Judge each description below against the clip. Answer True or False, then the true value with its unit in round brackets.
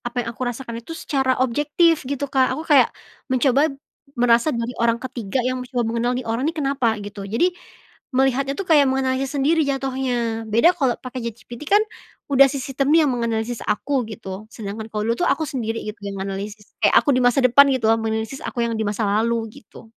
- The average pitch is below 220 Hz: False (250 Hz)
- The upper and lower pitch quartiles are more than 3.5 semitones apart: False (3.2 semitones)